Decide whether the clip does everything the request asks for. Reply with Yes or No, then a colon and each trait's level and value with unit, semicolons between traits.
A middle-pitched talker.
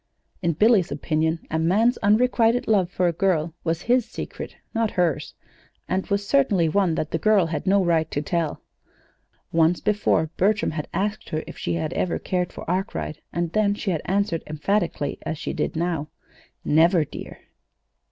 Yes: medium, 175 Hz